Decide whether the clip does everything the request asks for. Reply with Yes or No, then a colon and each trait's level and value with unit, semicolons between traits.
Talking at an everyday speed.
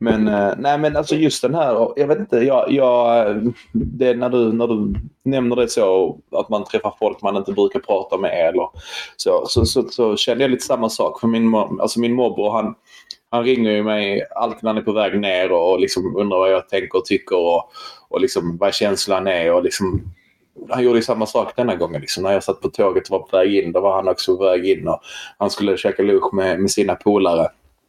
No: fast, 230 wpm